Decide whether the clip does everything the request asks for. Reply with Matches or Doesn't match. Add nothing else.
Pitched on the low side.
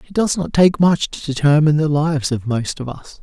Doesn't match